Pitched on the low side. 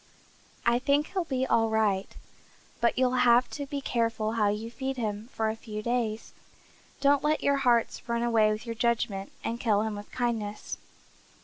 No: high, 235 Hz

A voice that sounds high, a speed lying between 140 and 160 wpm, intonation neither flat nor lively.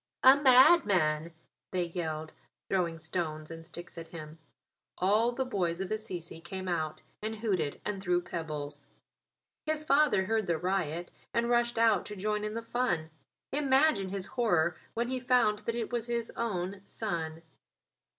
No: high, 195 Hz; average, 155 wpm; wide, 5.7 semitones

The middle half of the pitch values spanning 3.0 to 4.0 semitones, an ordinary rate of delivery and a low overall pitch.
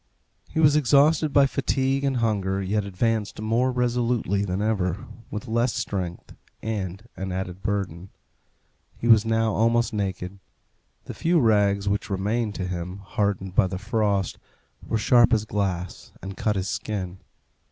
Yes: average, 3.6 semitones; average, 150 wpm; low, 105 Hz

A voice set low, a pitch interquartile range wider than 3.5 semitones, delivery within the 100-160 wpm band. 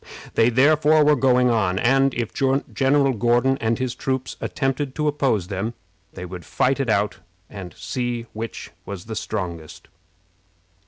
Yes: low, 120 Hz; average, 4.0 semitones; average, 150 wpm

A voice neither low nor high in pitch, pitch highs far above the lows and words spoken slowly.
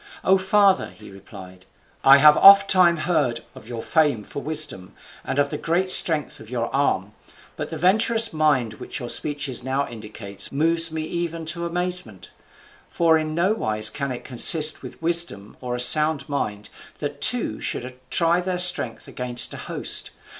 No: medium, 150 Hz; wide, 6.1 semitones; average, 165 wpm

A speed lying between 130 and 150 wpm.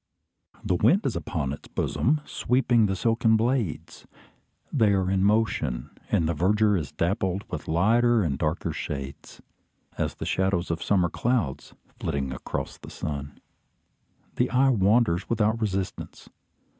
Yes: average, 140 wpm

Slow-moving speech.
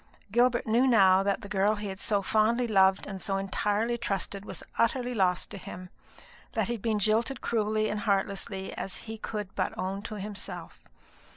No: average, 185 wpm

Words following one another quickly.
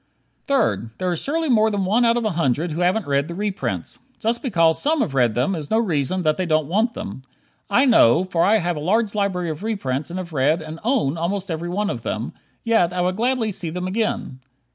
Yes: fast, 230 wpm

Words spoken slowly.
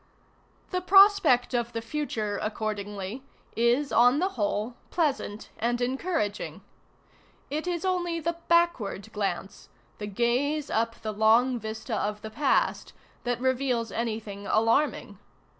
Yes: slow, 125 wpm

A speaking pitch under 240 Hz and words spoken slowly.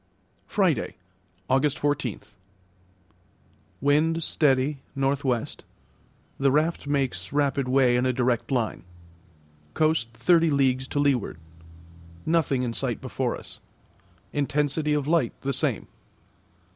Yes: medium, 140 Hz; slow, 105 wpm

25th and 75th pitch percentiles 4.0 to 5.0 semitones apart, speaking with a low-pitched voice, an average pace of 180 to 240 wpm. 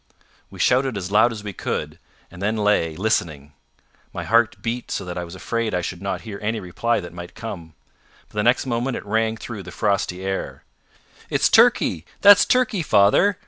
Yes: average, 4.4 semitones; low, 105 Hz; average, 190 wpm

